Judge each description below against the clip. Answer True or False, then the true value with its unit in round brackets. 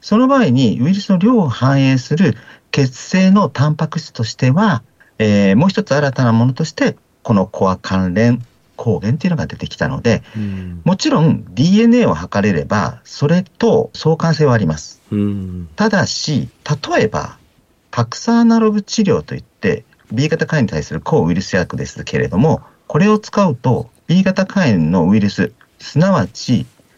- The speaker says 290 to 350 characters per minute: True (315 characters per minute)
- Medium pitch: True (145 Hz)